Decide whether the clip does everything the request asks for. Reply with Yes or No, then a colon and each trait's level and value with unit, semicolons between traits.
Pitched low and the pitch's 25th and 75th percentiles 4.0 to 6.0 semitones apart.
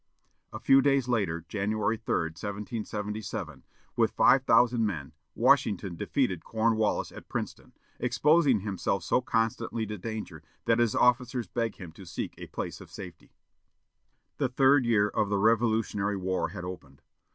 No: low, 110 Hz; average, 3.5 semitones